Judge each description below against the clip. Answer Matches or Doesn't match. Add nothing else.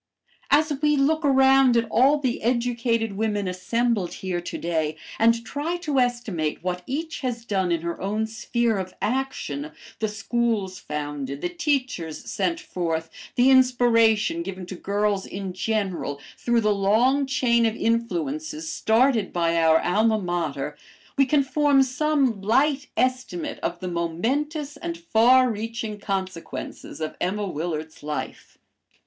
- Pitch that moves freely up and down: Matches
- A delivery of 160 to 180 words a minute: Doesn't match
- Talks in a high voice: Matches